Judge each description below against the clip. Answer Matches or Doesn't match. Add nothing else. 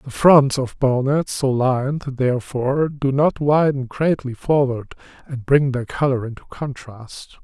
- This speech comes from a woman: Doesn't match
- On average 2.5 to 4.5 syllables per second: Matches